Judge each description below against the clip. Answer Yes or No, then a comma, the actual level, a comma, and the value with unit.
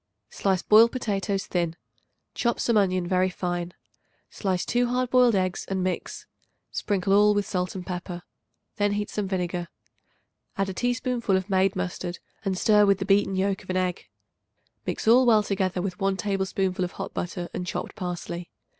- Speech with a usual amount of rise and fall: No, narrow, 2.3 semitones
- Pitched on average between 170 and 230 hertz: Yes, high, 190 Hz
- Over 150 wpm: Yes, average, 170 wpm